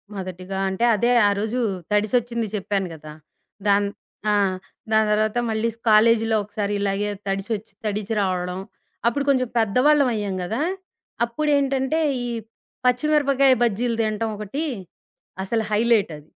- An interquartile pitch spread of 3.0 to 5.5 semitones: Yes, average, 3.4 semitones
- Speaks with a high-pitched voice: Yes, high, 220 Hz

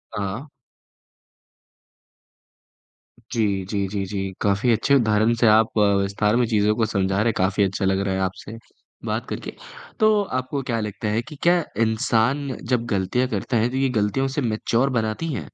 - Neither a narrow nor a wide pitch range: Yes, average, 3.8 semitones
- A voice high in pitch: No, low, 110 Hz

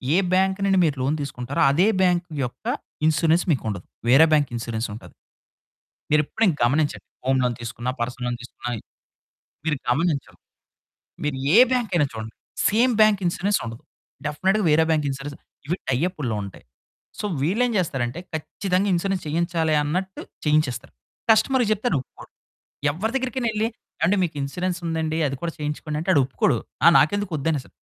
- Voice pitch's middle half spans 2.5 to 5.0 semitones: No, wide, 5.6 semitones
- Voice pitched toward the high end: No, medium, 155 Hz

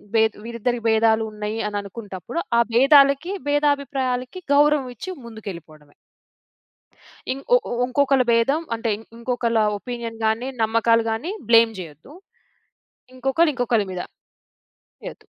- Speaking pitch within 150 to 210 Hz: No, high, 235 Hz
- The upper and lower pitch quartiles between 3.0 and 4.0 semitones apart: Yes, average, 3.5 semitones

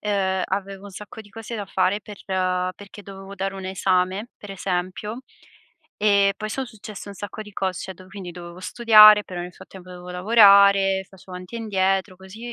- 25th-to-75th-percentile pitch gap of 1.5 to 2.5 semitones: Yes, narrow, 1.9 semitones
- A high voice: Yes, high, 195 Hz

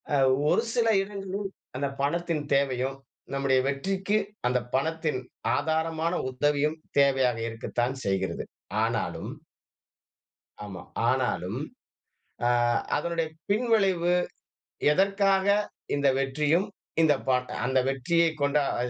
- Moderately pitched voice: Yes, medium, 150 Hz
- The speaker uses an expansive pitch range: No, average, 4.6 semitones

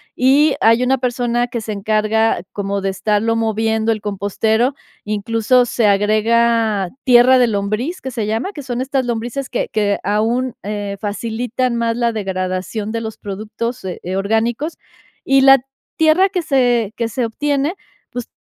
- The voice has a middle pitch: No, high, 230 Hz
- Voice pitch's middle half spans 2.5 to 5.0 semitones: Yes, average, 3.0 semitones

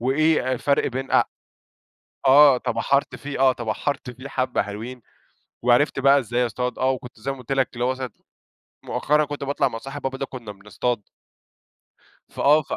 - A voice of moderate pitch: No, low, 130 Hz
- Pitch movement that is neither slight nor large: No, narrow, 2.1 semitones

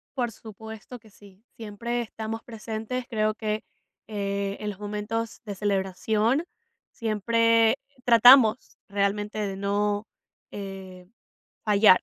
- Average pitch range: No, narrow, 2.0 semitones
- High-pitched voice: Yes, high, 215 Hz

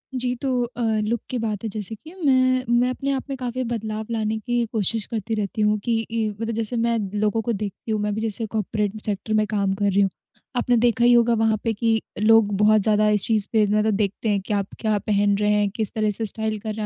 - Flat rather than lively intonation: Yes, narrow, 1.9 semitones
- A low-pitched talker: No, high, 220 Hz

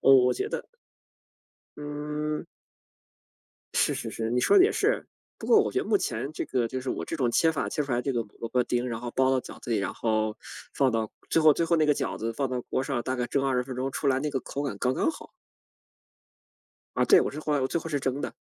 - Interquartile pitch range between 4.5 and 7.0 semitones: No, average, 3.3 semitones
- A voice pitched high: No, low, 135 Hz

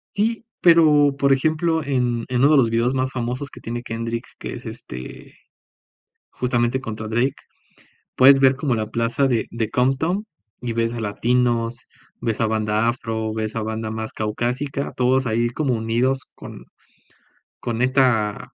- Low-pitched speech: Yes, low, 120 Hz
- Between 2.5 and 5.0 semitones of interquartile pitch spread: Yes, average, 2.9 semitones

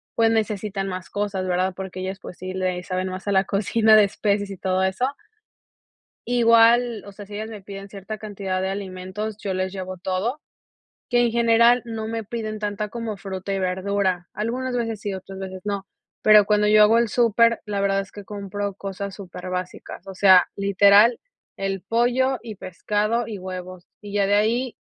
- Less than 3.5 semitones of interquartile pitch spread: Yes, narrow, 2.6 semitones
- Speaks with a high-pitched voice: Yes, high, 200 Hz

